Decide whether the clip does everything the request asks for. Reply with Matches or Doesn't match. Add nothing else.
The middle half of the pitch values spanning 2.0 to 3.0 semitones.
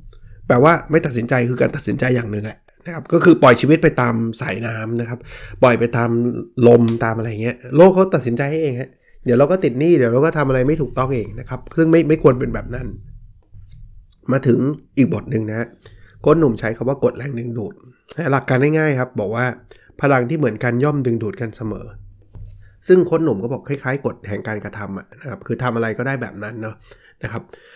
Doesn't match